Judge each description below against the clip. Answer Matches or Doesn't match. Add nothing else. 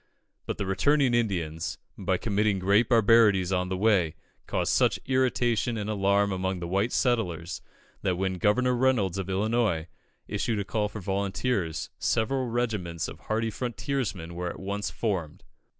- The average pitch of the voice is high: Doesn't match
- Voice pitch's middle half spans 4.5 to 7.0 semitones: Doesn't match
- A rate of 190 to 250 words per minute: Doesn't match